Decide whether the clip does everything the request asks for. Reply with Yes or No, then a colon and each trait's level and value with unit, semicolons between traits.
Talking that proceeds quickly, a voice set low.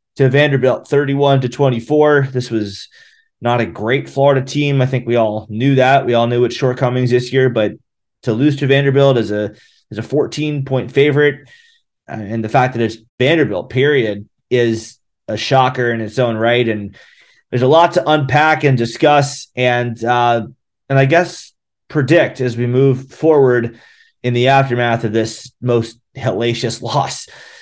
No: average, 165 wpm; low, 125 Hz